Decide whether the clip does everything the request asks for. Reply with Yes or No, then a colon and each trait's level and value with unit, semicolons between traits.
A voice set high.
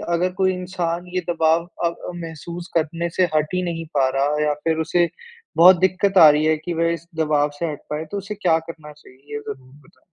No: medium, 165 Hz